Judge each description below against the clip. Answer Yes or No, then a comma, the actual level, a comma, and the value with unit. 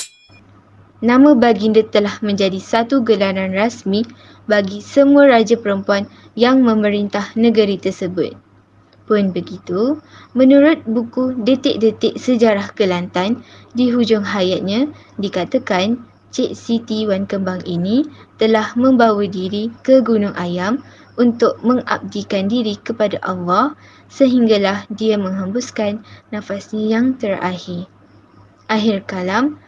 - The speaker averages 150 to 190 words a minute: No, average, 100 wpm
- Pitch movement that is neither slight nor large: Yes, average, 3.7 semitones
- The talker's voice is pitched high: Yes, high, 215 Hz